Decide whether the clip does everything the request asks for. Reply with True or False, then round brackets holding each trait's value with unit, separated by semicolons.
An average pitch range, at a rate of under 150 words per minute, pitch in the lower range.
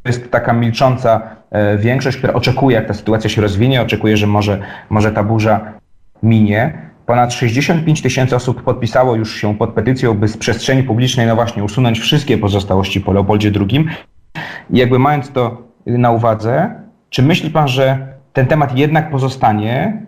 False (3.6 semitones; 160 wpm; 120 Hz)